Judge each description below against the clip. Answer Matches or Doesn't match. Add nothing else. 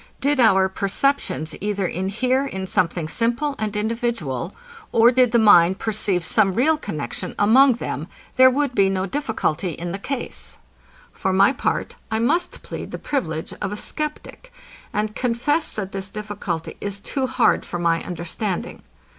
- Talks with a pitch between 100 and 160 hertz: Doesn't match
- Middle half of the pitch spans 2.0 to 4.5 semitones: Doesn't match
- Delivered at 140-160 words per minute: Matches